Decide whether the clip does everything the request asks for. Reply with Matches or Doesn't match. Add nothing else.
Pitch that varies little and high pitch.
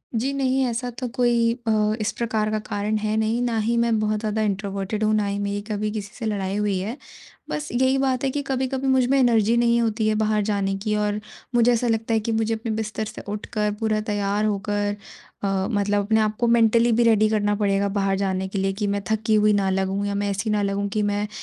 Matches